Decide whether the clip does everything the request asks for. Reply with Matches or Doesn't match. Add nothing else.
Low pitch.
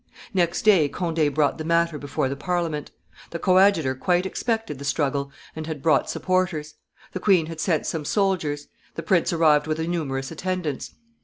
Doesn't match